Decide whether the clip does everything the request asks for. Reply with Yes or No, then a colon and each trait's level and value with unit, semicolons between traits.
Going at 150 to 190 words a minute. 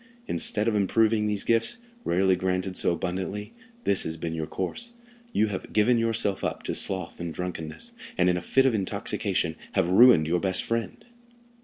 Yes: average, 170 wpm